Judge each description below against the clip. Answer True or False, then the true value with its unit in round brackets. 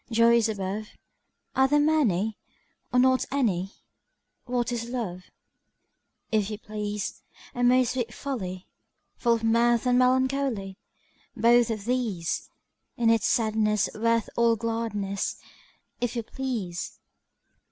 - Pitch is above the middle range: True (230 Hz)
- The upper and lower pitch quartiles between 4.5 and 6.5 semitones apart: False (2.8 semitones)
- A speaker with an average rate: False (120 wpm)